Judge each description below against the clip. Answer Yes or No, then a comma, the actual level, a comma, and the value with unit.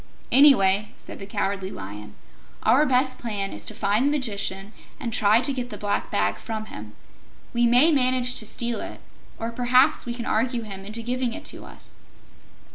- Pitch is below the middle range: No, high, 230 Hz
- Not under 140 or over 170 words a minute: No, average, 185 wpm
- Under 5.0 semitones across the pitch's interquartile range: Yes, average, 4.0 semitones